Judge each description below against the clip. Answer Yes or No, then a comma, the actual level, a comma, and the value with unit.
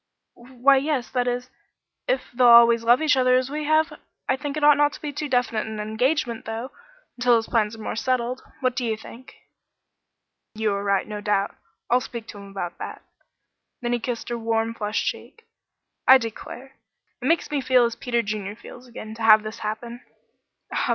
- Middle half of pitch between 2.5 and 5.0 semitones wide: Yes, average, 2.9 semitones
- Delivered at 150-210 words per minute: Yes, average, 195 wpm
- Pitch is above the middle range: Yes, high, 240 Hz